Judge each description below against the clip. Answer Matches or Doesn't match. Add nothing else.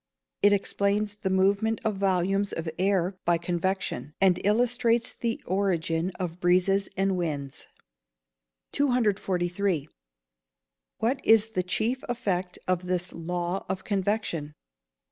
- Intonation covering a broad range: Doesn't match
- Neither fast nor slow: Doesn't match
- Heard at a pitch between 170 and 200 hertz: Matches